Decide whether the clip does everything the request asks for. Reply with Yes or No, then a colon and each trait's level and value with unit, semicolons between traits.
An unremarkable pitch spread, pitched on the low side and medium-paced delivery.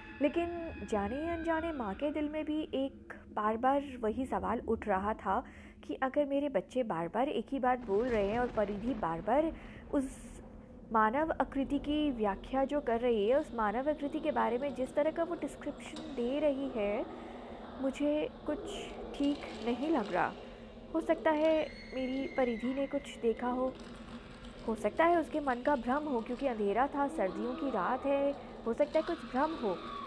No: average, 3.8 semitones; very high, 265 Hz; average, 180 wpm